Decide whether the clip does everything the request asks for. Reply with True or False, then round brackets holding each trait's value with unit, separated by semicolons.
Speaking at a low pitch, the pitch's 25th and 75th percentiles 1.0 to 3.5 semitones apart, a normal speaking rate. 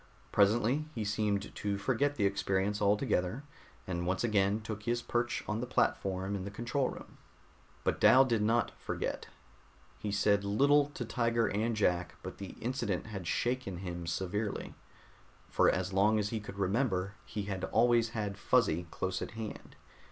True (105 Hz; 3.2 semitones; 165 wpm)